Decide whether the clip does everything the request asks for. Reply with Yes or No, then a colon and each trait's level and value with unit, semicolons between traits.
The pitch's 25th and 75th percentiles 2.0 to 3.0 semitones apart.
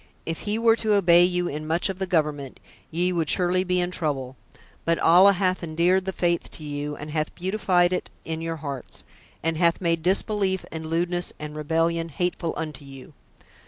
Yes: narrow, 2.6 semitones